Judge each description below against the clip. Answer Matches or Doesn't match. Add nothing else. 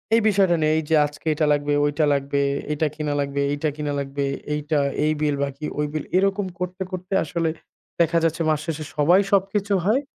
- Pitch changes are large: Doesn't match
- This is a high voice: Doesn't match